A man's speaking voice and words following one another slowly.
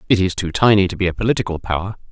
No: male; fast, 255 wpm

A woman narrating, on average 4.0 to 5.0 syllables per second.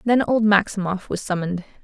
No: female; 5.7 syllables/s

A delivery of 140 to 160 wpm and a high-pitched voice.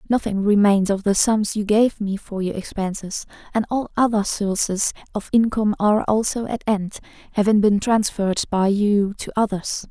No: average, 170 wpm; high, 205 Hz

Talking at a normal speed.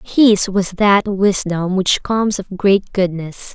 Yes: average, 150 wpm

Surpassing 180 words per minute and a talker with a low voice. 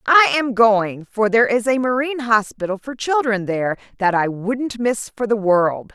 No: average, 190 wpm; high, 225 Hz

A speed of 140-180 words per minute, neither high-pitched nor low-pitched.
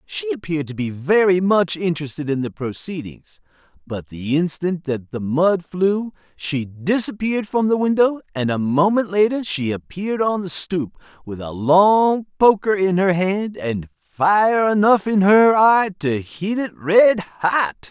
Yes: average, 165 wpm; medium, 175 Hz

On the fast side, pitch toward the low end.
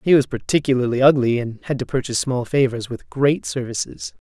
No: average, 180 wpm; low, 130 Hz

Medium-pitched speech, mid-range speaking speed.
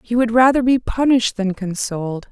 No: high, 225 Hz; average, 180 wpm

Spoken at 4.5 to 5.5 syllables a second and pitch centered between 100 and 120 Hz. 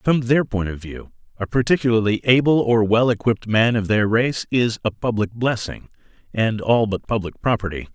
Yes: 5.2 syllables/s; low, 115 Hz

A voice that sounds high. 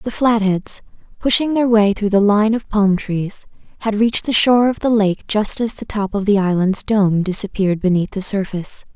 Yes: high, 205 Hz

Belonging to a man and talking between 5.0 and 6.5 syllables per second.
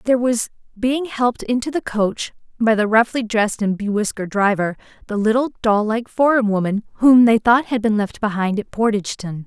No: female; 5.5 syllables/s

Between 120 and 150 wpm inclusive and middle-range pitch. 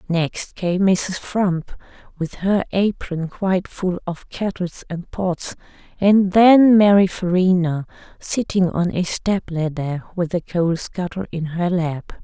Yes: average, 140 wpm; medium, 180 Hz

